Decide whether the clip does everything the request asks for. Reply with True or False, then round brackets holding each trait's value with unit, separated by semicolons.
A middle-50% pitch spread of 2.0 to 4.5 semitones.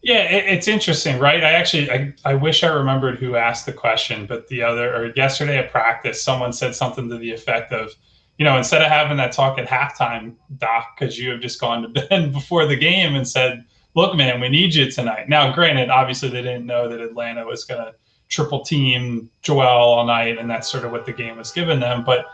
True (3.8 semitones)